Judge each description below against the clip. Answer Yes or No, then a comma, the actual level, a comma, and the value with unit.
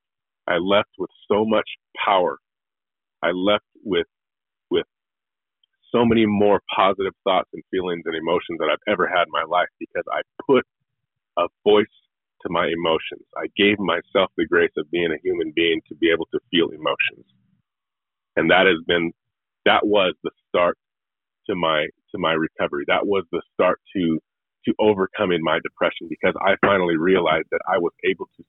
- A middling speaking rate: Yes, average, 170 wpm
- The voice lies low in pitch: No, very high, 310 Hz